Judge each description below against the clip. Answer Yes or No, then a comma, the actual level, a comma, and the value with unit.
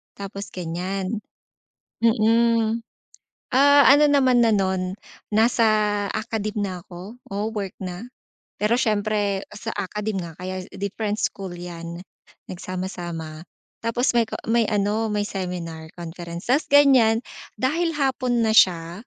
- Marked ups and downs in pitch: No, average, 4.0 semitones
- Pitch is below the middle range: No, high, 205 Hz